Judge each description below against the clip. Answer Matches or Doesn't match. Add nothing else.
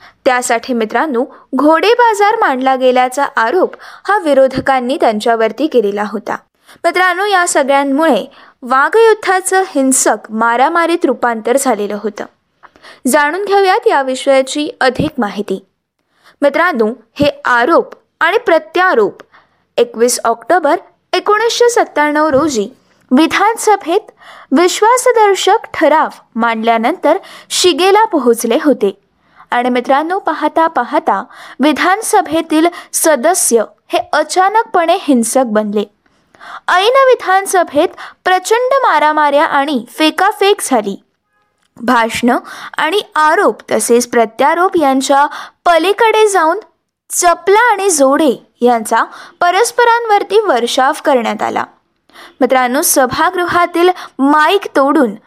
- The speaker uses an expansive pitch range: Matches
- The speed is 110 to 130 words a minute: Doesn't match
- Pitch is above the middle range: Matches